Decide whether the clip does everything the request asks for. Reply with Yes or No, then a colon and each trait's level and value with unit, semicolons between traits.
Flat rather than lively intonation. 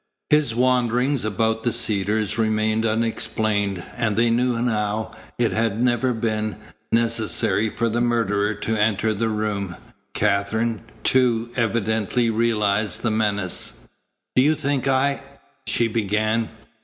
Yes: narrow, 1.8 semitones